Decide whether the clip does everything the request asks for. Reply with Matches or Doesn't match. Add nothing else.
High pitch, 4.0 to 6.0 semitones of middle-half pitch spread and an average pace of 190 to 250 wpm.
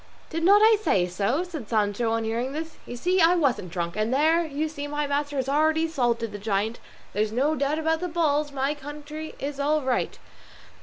Matches